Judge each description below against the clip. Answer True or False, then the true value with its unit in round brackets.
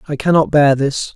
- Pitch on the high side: False (145 Hz)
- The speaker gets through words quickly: True (210 wpm)